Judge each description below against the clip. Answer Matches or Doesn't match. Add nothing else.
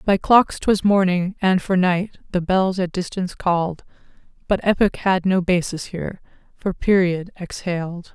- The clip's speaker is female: Matches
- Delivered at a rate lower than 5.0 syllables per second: Matches